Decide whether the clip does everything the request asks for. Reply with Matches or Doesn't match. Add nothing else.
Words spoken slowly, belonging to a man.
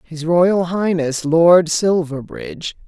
Doesn't match